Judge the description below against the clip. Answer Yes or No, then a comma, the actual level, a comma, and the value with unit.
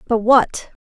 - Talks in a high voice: Yes, high, 230 Hz